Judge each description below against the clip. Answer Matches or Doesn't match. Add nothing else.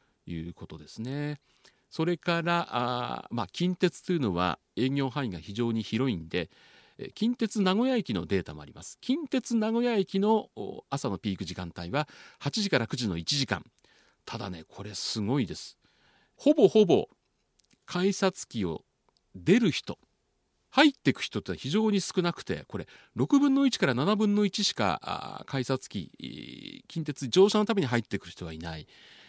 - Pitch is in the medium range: Matches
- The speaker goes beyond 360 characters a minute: Doesn't match